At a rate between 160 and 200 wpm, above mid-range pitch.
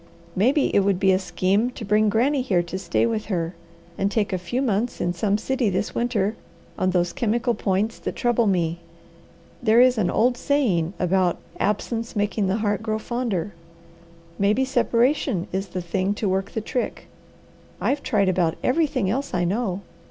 Yes: average, 175 wpm; high, 210 Hz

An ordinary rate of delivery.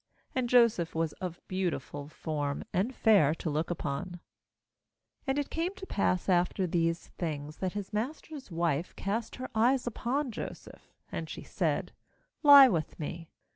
Yes: average, 155 wpm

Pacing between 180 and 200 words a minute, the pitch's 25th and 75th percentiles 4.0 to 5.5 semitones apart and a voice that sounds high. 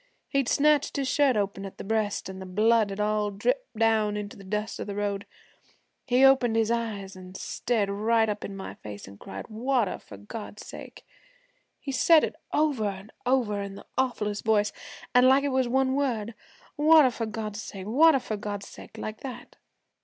Yes: average, 190 wpm; average, 4.3 semitones; high, 220 Hz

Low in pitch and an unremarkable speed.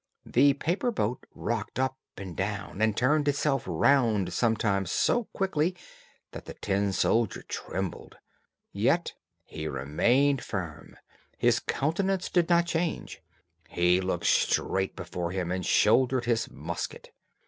No: low, 115 Hz; slow, 125 wpm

